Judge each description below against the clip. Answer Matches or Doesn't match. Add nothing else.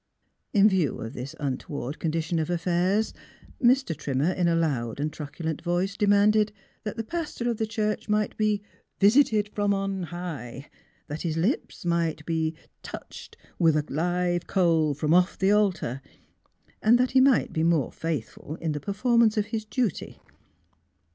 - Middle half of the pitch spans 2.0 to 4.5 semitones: Doesn't match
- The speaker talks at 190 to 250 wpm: Doesn't match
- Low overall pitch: Doesn't match